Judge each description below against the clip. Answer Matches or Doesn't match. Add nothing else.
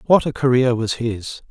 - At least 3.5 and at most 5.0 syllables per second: Matches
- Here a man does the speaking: Matches